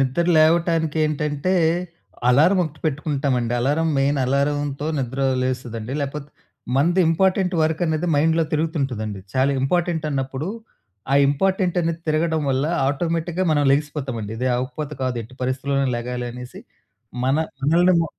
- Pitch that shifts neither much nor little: Yes, average, 3.6 semitones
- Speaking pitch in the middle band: Yes, medium, 145 Hz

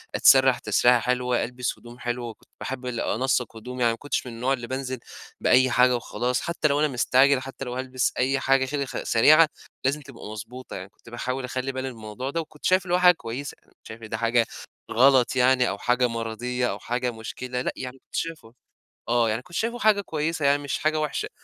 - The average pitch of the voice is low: Yes, low, 125 Hz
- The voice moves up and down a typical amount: No, narrow, 2.3 semitones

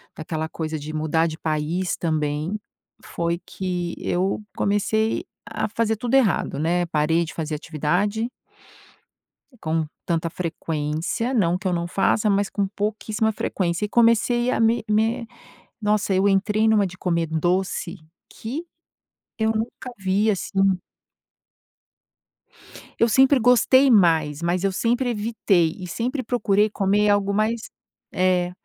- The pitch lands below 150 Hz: No, high, 195 Hz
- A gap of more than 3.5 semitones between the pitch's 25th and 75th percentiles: Yes, average, 4.6 semitones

